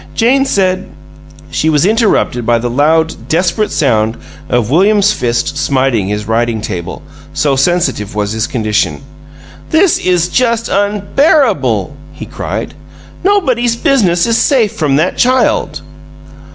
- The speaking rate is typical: No, slow, 130 wpm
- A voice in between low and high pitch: Yes, medium, 160 Hz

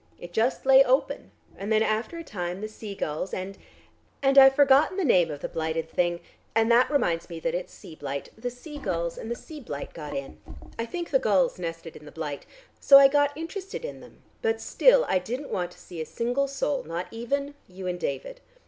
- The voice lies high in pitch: Yes, high, 220 Hz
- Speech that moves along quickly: Yes, fast, 220 wpm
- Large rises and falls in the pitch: Yes, wide, 8.2 semitones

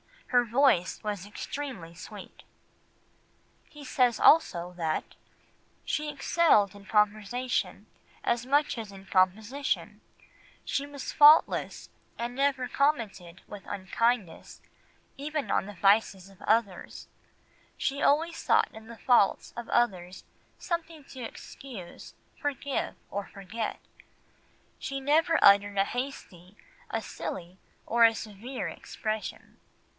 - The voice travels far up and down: Yes, wide, 5.7 semitones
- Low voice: No, high, 230 Hz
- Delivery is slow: Yes, slow, 115 wpm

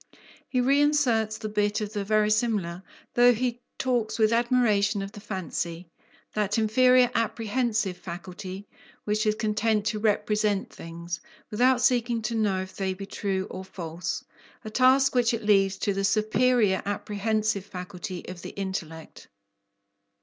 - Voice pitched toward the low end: No, high, 210 Hz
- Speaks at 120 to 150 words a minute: Yes, average, 140 wpm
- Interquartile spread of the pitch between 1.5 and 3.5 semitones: Yes, average, 3.1 semitones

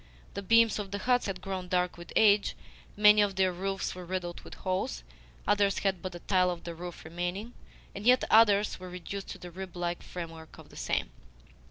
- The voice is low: No, medium, 185 Hz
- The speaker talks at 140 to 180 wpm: No, fast, 205 wpm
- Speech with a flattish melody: Yes, narrow, 2.3 semitones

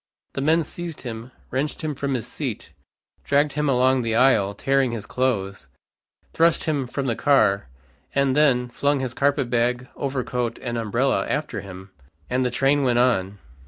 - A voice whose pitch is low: Yes, low, 130 Hz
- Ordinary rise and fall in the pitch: Yes, average, 3.0 semitones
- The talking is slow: No, average, 165 wpm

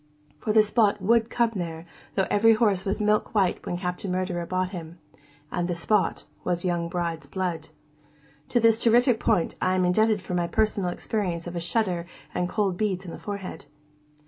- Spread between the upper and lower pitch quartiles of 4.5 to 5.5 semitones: No, average, 3.4 semitones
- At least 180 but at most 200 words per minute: Yes, average, 190 wpm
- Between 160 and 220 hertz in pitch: Yes, medium, 185 Hz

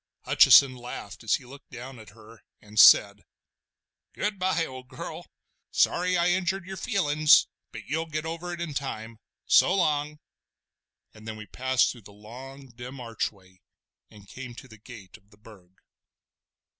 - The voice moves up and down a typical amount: No, wide, 6.2 semitones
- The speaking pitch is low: Yes, low, 125 Hz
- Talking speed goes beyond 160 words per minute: No, average, 155 wpm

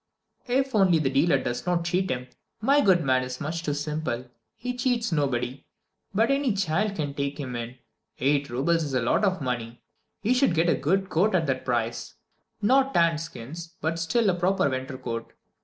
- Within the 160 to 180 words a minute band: No, average, 190 wpm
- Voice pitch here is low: No, medium, 160 Hz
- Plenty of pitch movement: Yes, wide, 6.7 semitones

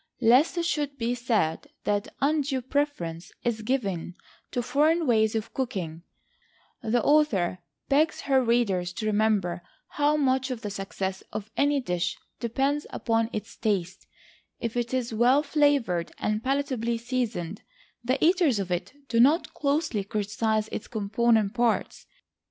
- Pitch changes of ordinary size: Yes, average, 4.9 semitones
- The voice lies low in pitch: No, high, 235 Hz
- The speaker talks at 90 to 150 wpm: Yes, average, 140 wpm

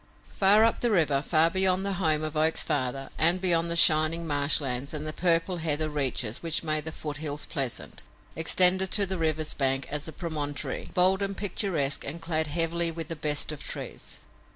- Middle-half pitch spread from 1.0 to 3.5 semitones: Yes, average, 3.0 semitones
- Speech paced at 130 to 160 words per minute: No, average, 180 wpm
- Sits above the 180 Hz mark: No, medium, 160 Hz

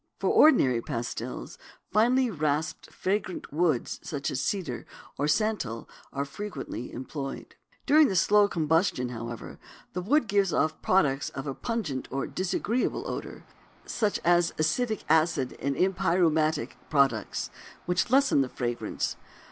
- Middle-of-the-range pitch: Yes, medium, 160 Hz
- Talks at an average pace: No, slow, 130 wpm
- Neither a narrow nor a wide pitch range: No, wide, 6.8 semitones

